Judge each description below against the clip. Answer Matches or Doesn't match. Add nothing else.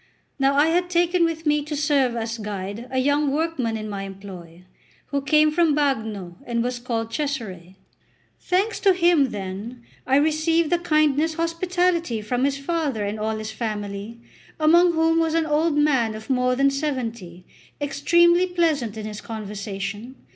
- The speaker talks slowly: Doesn't match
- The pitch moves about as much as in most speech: Doesn't match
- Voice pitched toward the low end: Doesn't match